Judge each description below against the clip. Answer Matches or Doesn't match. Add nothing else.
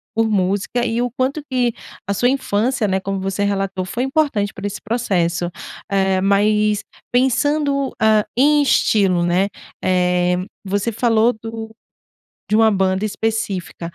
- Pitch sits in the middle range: Doesn't match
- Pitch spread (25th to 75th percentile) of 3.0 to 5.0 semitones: Matches